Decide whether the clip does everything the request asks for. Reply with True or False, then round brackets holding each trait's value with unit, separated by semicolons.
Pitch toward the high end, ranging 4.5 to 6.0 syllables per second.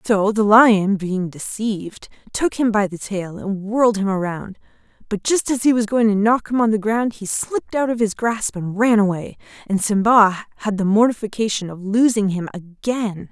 True (210 Hz; 4.8 syllables/s)